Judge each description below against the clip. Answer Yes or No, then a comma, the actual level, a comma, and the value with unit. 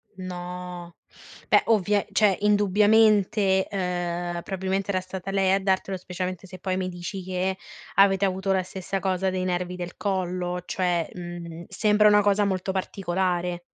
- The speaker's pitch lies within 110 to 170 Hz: No, medium, 185 Hz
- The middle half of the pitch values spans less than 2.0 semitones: Yes, narrow, 1.6 semitones